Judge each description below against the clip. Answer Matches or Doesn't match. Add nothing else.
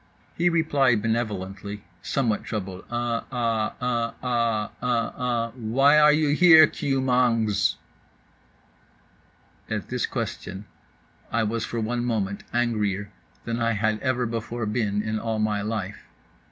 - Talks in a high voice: Doesn't match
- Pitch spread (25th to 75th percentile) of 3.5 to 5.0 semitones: Doesn't match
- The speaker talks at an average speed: Doesn't match